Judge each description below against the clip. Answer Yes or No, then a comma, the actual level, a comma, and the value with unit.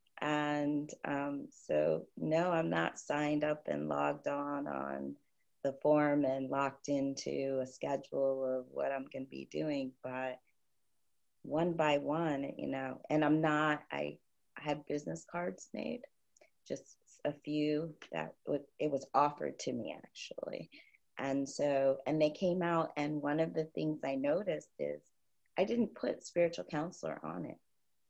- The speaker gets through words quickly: No, average, 155 wpm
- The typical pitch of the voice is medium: Yes, medium, 145 Hz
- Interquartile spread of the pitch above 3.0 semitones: No, narrow, 2.4 semitones